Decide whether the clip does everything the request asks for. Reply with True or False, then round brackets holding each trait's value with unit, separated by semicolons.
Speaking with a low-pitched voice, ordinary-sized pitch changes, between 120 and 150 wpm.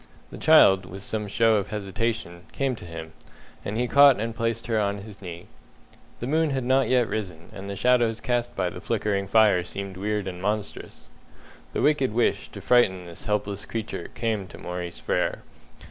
False (105 Hz; 3.4 semitones; 185 wpm)